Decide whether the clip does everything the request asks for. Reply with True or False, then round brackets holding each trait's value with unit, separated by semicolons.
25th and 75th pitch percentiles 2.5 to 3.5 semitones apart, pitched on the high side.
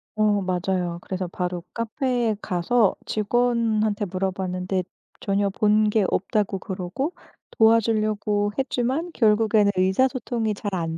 True (3.2 semitones; 210 Hz)